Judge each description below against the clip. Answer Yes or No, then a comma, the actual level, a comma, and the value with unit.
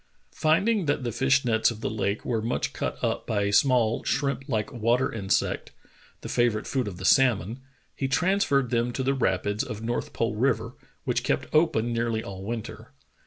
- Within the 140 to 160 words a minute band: No, average, 185 wpm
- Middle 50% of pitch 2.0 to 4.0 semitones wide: Yes, average, 3.5 semitones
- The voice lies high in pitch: No, low, 120 Hz